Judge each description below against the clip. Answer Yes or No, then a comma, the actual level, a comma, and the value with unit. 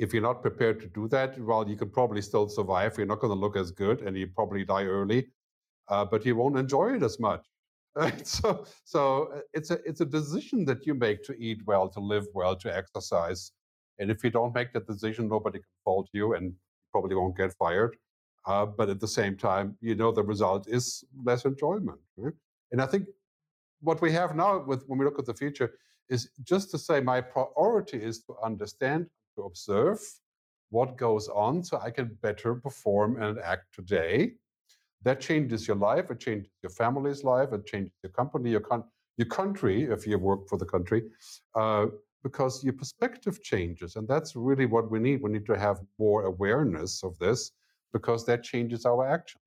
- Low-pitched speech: Yes, low, 115 Hz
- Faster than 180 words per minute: Yes, average, 200 wpm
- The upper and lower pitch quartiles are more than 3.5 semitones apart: Yes, average, 4.4 semitones